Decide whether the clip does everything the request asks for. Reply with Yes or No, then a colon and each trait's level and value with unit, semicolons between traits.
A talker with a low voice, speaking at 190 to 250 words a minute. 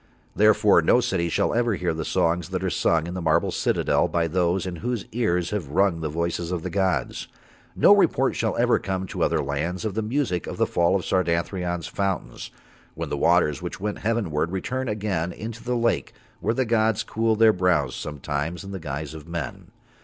Yes: very low, 90 Hz; average, 200 wpm